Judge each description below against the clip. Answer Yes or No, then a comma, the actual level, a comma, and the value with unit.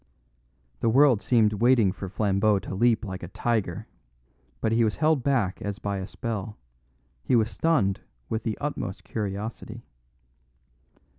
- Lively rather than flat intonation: No, average, 3.2 semitones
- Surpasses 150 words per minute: No, average, 145 wpm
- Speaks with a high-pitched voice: No, low, 110 Hz